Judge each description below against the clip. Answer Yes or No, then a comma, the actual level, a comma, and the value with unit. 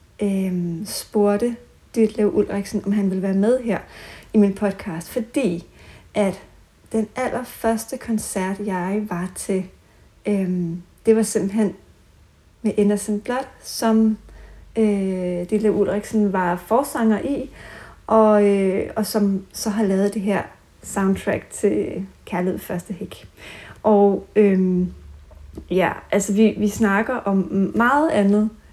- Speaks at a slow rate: Yes, slow, 125 wpm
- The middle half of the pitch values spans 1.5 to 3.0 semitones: Yes, narrow, 2.5 semitones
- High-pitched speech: Yes, high, 205 Hz